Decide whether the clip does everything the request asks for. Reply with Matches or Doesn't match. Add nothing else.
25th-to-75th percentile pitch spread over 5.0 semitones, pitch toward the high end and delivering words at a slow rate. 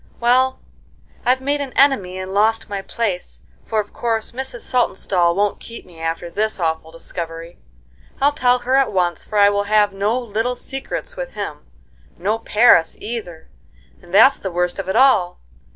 Doesn't match